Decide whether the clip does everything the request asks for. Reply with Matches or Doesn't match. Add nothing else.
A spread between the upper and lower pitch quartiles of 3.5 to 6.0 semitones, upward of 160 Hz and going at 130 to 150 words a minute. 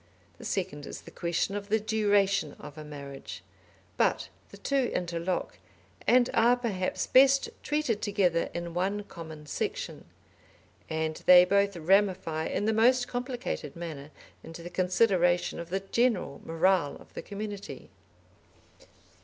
Matches